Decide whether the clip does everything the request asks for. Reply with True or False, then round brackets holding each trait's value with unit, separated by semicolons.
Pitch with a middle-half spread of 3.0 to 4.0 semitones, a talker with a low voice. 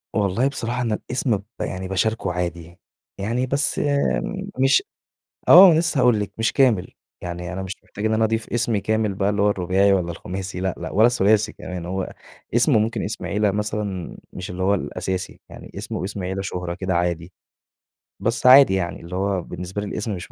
True (3.4 semitones; 100 Hz)